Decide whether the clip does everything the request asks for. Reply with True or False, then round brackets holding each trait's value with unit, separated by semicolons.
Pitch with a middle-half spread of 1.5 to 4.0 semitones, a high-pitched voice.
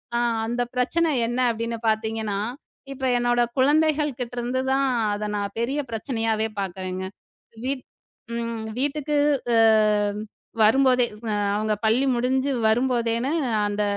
True (3.2 semitones; 240 Hz)